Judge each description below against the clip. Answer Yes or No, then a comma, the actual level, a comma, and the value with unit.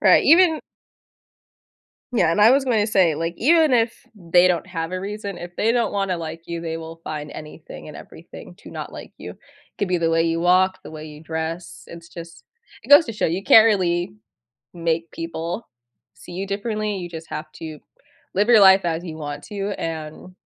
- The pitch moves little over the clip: No, average, 4.0 semitones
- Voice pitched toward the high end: No, medium, 175 Hz